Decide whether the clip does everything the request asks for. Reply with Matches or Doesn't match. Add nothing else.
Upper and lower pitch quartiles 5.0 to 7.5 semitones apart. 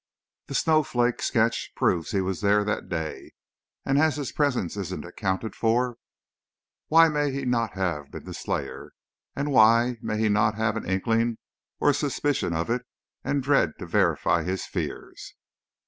Matches